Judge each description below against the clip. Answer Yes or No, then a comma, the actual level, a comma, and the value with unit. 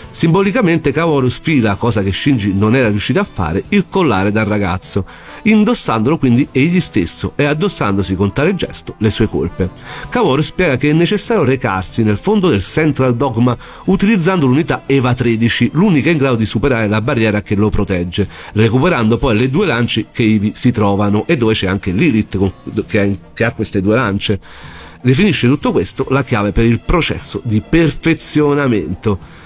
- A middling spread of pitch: No, wide, 6.1 semitones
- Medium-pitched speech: No, low, 120 Hz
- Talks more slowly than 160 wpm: No, average, 165 wpm